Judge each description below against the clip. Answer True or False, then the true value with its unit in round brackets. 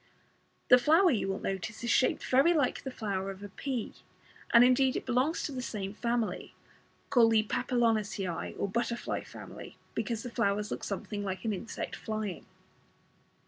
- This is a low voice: False (230 Hz)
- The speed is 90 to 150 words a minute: False (165 wpm)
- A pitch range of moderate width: True (3.7 semitones)